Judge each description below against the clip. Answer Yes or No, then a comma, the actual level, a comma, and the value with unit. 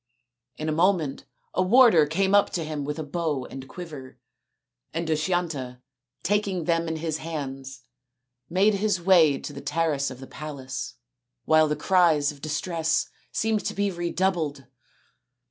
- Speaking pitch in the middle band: Yes, medium, 160 Hz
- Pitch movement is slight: No, average, 3.7 semitones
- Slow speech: No, average, 150 wpm